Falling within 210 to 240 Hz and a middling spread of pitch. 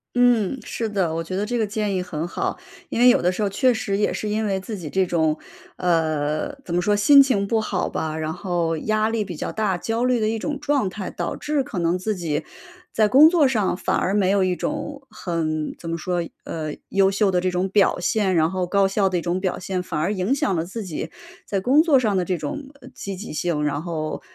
No: high, 195 Hz; average, 4.1 semitones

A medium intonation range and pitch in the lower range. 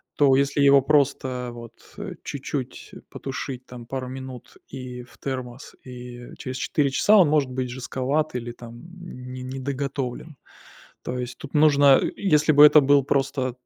No: narrow, 2.1 semitones; low, 130 Hz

